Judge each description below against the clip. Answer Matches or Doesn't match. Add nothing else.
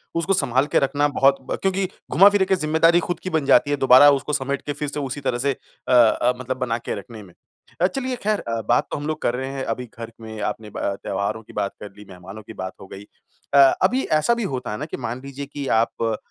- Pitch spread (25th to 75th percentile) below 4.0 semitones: Doesn't match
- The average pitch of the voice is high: Doesn't match